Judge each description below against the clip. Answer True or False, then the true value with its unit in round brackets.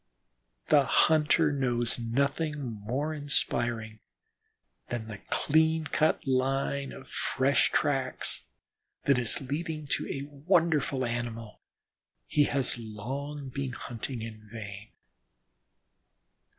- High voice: False (135 Hz)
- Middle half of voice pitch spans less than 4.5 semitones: True (3.9 semitones)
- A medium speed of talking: False (100 wpm)